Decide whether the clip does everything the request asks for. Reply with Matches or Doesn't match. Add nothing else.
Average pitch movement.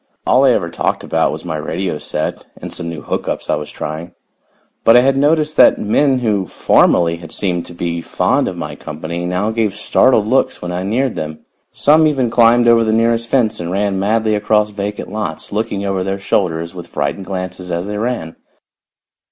Matches